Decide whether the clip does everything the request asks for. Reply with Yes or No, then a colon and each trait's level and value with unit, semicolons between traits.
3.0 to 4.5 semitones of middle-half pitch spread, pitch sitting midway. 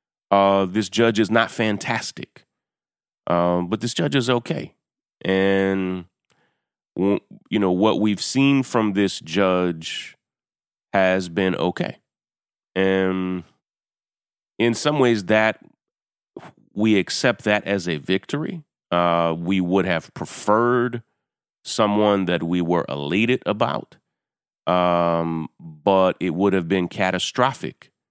No: average, 3.5 semitones; very low, 95 Hz